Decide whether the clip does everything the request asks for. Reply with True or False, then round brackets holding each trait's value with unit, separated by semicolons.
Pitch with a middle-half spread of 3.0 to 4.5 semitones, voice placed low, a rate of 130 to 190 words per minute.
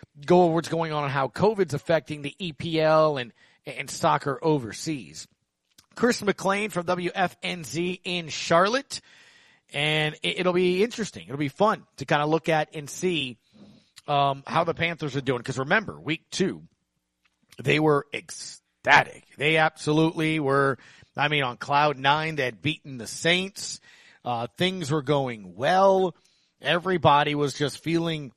False (4.0 semitones; 155 Hz; 150 wpm)